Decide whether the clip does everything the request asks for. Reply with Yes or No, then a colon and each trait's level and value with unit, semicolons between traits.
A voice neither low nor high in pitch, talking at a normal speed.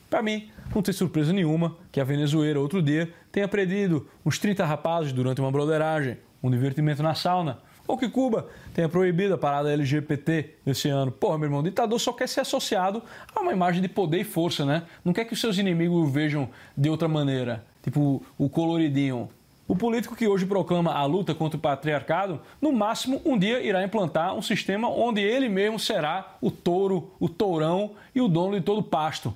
No: medium, 170 Hz; fast, 200 wpm